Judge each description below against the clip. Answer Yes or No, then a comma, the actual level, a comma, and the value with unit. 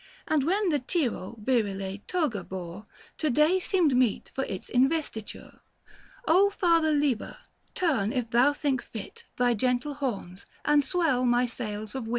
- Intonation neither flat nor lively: No, wide, 5.7 semitones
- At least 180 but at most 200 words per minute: No, average, 160 wpm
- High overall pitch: Yes, very high, 255 Hz